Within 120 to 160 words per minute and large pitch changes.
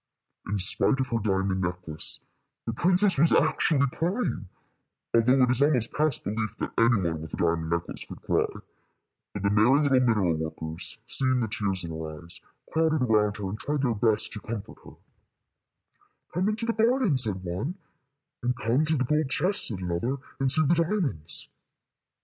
No: average, 180 wpm; wide, 7.6 semitones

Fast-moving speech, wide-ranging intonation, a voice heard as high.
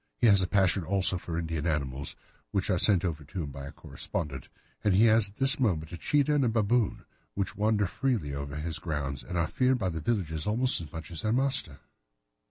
No: fast, 220 wpm; wide, 5.9 semitones; very low, 90 Hz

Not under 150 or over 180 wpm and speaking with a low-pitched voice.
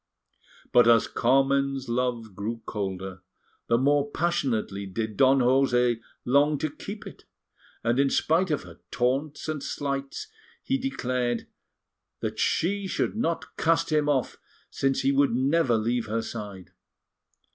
No: slow, 135 wpm; low, 130 Hz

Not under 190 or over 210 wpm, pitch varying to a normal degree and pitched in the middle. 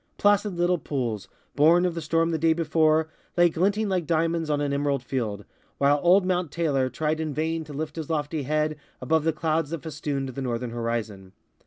Yes: average, 195 wpm; average, 3.0 semitones; medium, 155 Hz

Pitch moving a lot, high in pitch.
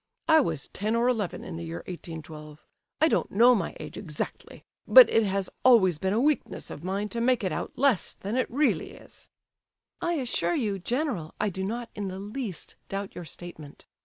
Yes: wide, 5.9 semitones; high, 200 Hz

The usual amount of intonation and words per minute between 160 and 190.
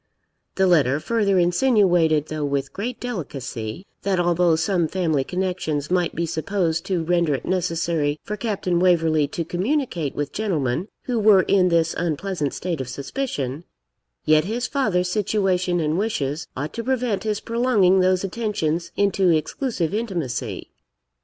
No: average, 4.4 semitones; average, 145 wpm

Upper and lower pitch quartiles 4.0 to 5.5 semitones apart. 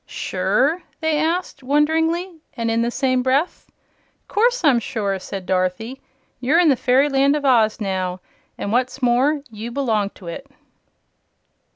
Yes: average, 5.1 semitones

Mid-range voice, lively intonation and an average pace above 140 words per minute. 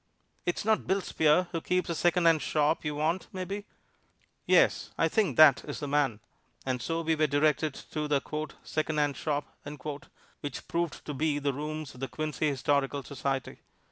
No: medium, 150 Hz; narrow, 2.5 semitones; average, 170 wpm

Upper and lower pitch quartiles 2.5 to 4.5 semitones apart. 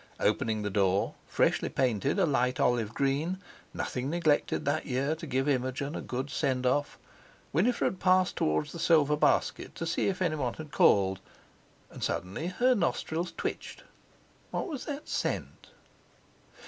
No: average, 5.0 semitones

